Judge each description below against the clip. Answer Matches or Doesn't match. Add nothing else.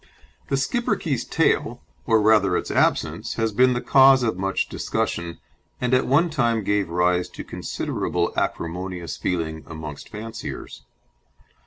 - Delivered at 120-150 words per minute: Matches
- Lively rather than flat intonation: Matches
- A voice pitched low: Matches